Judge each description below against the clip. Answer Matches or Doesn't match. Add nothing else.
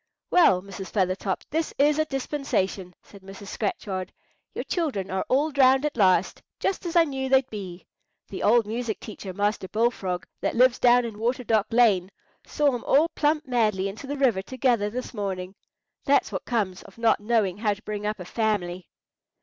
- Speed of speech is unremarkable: Matches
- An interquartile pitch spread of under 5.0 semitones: Doesn't match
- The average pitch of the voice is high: Matches